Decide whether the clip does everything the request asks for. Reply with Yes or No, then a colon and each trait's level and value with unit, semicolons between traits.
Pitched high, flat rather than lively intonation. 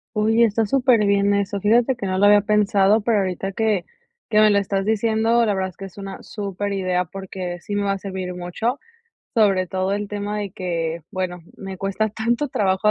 Yes: high, 200 Hz; narrow, 2.2 semitones